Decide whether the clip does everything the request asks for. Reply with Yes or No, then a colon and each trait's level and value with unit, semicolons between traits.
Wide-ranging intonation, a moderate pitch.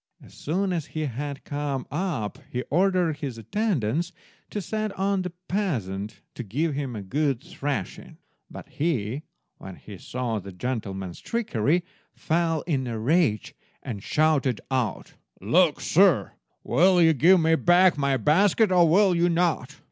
Yes: wide, 6.3 semitones; medium, 150 Hz